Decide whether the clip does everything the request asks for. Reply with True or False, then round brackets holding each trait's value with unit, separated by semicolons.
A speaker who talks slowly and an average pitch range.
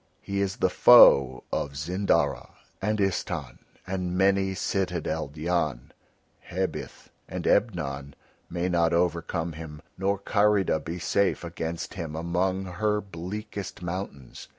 True (120 wpm; 3.2 semitones)